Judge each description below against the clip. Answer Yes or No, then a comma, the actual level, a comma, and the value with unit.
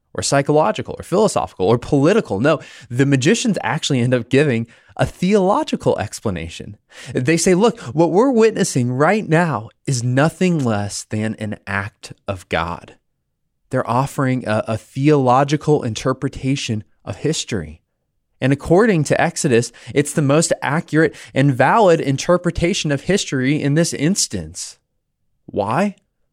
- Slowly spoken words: Yes, slow, 130 wpm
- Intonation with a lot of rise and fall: Yes, wide, 5.9 semitones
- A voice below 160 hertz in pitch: Yes, medium, 140 Hz